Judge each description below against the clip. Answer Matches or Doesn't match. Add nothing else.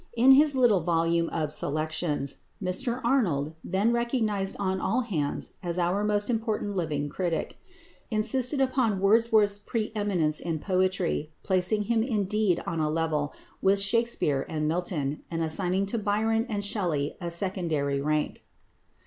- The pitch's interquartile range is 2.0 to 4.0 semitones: Doesn't match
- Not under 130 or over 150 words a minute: Matches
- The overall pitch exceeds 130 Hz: Matches